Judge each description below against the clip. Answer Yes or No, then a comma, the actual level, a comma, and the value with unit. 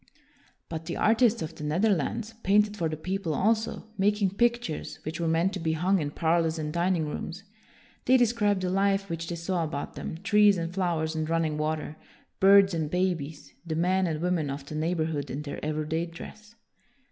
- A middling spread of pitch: Yes, average, 3.8 semitones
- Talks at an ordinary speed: Yes, average, 190 wpm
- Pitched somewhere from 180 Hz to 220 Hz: No, medium, 170 Hz